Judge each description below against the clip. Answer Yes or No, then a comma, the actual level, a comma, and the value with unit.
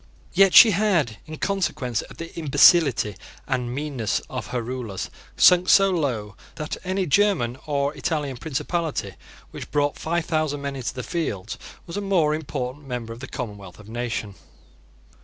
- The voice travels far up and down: Yes, wide, 5.8 semitones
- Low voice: No, medium, 145 Hz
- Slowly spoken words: No, average, 160 wpm